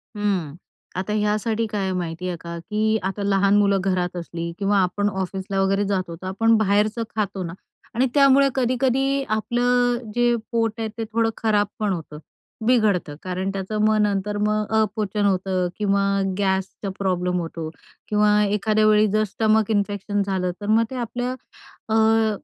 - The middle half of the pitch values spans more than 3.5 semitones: No, narrow, 2.5 semitones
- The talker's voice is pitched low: No, high, 205 Hz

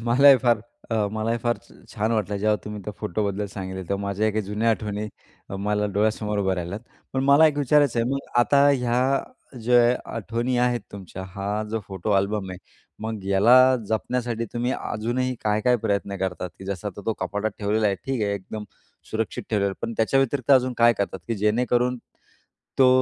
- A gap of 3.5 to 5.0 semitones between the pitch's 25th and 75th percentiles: No, average, 3.1 semitones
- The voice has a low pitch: Yes, low, 110 Hz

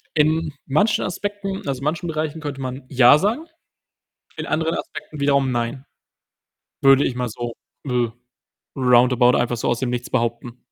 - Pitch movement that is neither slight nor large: Yes, average, 4.2 semitones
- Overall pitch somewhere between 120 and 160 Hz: Yes, low, 135 Hz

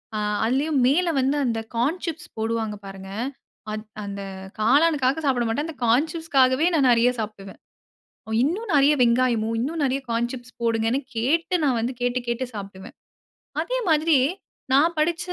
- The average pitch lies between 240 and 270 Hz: Yes, very high, 255 Hz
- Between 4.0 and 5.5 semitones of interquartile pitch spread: Yes, average, 5.1 semitones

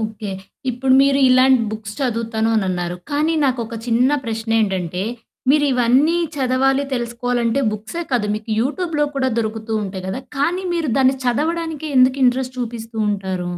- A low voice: No, high, 245 Hz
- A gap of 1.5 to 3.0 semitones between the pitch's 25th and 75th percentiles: No, average, 3.5 semitones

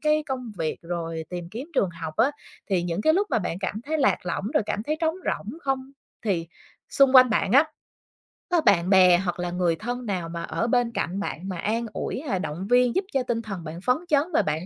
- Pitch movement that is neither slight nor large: No, wide, 6.7 semitones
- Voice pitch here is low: No, high, 205 Hz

